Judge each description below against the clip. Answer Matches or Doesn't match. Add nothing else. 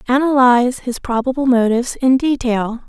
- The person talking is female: Matches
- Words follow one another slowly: Matches